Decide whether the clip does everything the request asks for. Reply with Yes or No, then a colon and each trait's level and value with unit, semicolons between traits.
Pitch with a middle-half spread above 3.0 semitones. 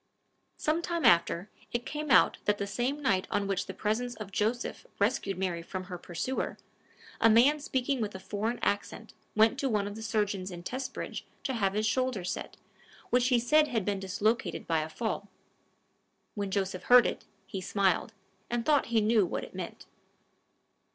Yes: average, 4.1 semitones